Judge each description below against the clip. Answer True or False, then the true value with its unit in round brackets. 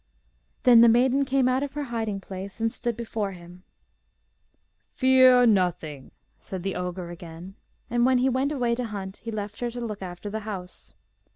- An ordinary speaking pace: True (180 wpm)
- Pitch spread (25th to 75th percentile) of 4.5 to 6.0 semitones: True (4.8 semitones)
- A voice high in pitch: True (220 Hz)